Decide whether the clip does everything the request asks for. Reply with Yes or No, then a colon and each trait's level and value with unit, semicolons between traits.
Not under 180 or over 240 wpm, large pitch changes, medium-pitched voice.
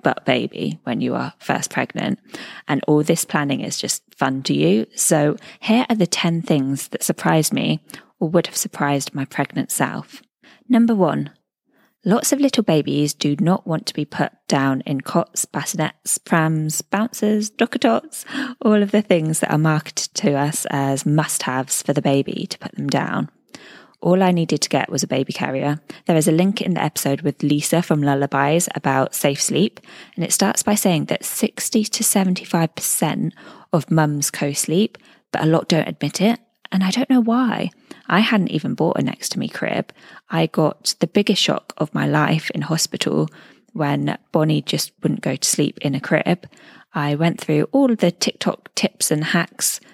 Yes: average, 185 wpm; wide, 6.4 semitones; medium, 170 Hz